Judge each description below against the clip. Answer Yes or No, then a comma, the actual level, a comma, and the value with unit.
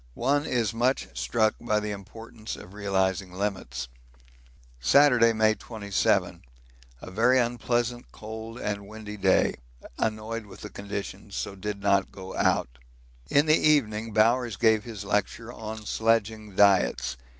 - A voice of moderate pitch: No, low, 110 Hz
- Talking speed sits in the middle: No, slow, 130 wpm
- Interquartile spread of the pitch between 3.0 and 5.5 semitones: No, narrow, 2.5 semitones